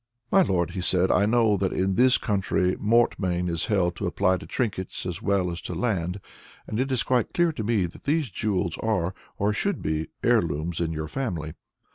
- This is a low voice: Yes, very low, 95 Hz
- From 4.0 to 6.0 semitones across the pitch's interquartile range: Yes, average, 4.5 semitones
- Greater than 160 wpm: Yes, average, 200 wpm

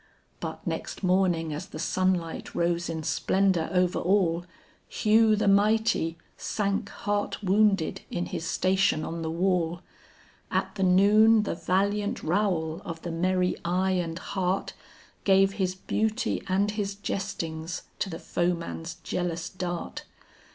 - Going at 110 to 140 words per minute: Yes, slow, 135 wpm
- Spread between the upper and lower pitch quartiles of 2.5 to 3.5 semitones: Yes, average, 2.9 semitones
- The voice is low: No, medium, 185 Hz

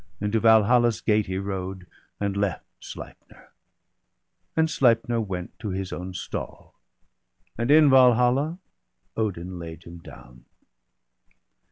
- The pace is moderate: No, slow, 120 wpm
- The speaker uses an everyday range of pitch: Yes, average, 4.5 semitones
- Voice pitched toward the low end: Yes, low, 105 Hz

